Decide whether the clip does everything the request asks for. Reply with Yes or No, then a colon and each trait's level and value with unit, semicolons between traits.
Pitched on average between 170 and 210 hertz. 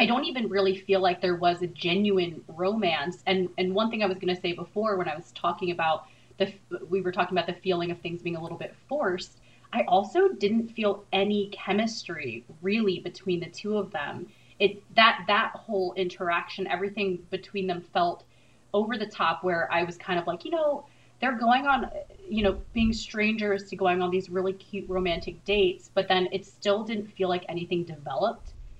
Yes: high, 190 Hz